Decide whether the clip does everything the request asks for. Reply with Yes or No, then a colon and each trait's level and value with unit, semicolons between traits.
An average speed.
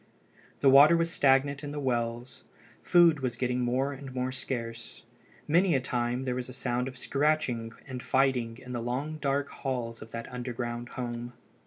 Yes: average, 175 wpm